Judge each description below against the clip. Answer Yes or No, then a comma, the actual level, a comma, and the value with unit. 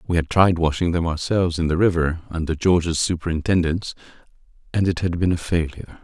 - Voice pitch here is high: No, very low, 85 Hz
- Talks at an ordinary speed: Yes, average, 180 wpm